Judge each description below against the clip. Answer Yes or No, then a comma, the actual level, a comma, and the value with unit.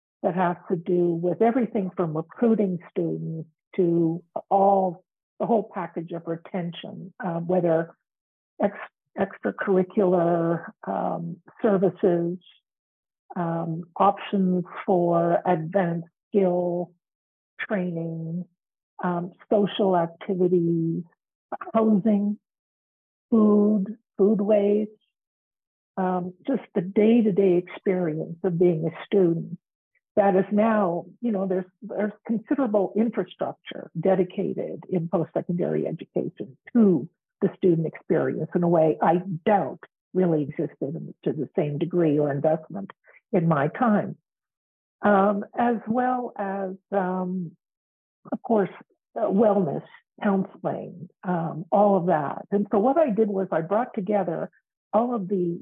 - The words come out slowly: Yes, slow, 115 wpm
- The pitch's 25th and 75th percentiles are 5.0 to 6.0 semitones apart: No, average, 3.2 semitones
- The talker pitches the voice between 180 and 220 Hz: Yes, medium, 185 Hz